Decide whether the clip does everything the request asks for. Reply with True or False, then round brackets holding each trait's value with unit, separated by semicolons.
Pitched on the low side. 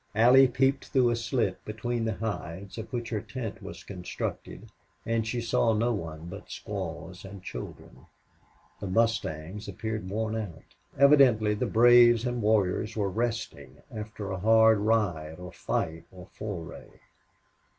True (110 Hz)